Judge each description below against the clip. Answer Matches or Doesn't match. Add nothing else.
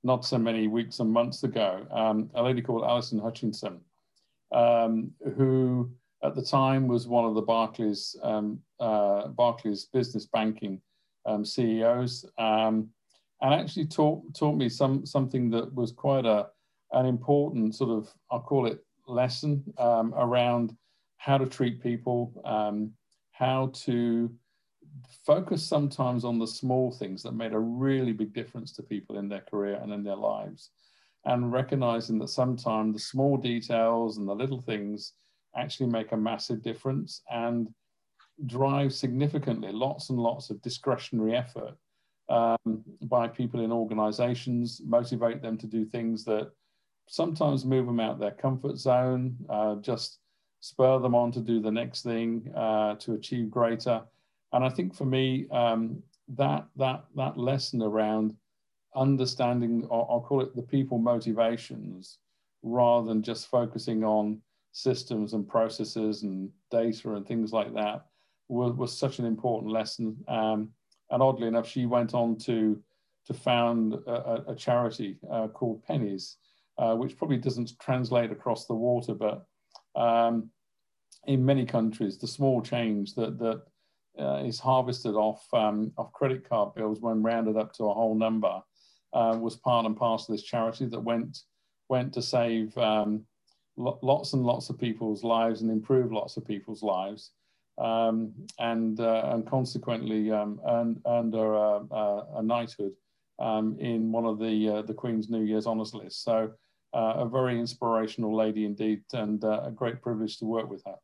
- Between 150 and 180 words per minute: Matches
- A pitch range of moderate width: Doesn't match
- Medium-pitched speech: Doesn't match